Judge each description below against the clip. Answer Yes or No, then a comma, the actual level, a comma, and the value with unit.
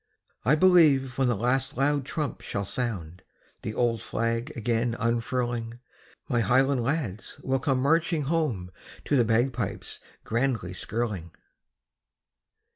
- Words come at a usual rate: No, slow, 120 wpm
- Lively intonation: No, average, 3.1 semitones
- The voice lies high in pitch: No, low, 120 Hz